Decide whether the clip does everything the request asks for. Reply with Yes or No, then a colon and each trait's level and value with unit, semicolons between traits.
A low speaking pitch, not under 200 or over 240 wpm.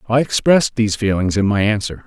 Yes: low, 110 Hz; fast, 205 wpm